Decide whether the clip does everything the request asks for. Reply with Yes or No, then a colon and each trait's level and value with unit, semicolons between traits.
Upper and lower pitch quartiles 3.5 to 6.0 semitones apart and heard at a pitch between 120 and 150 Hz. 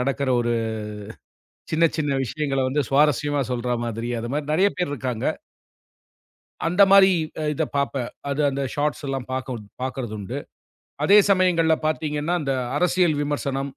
No: average, 3.1 semitones; medium, 140 Hz